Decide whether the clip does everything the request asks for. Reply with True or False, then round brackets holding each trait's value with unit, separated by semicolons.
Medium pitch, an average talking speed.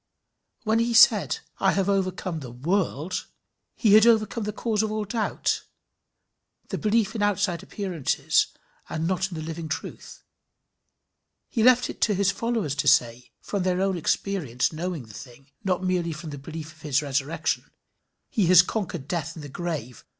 True (180 Hz; 170 wpm)